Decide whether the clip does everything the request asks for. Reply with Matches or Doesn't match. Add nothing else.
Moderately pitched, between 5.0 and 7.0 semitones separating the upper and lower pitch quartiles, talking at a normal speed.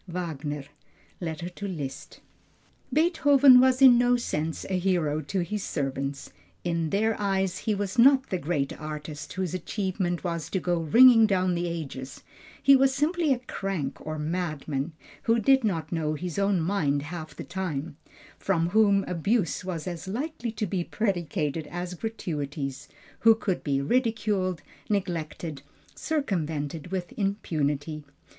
Matches